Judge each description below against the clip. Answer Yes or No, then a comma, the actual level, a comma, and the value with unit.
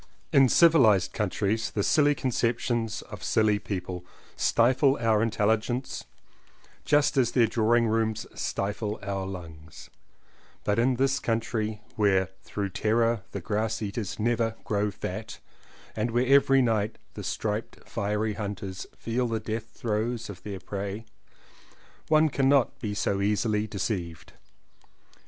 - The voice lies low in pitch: Yes, low, 110 Hz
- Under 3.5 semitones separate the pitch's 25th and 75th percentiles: Yes, narrow, 2.5 semitones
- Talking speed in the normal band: No, slow, 130 wpm